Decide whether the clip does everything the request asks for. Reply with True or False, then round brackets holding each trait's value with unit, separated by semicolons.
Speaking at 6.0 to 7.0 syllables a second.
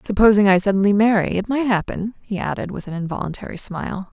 True (6.3 syllables/s)